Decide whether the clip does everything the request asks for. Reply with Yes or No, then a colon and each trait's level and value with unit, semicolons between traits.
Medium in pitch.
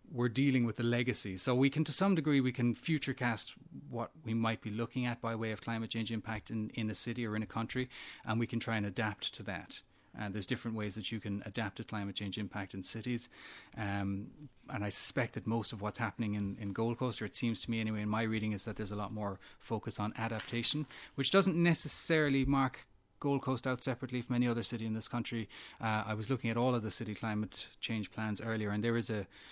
No: low, 115 Hz